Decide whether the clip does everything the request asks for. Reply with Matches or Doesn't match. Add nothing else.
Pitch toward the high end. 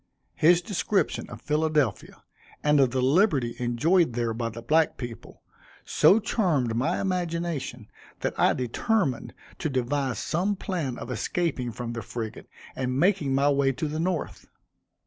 Doesn't match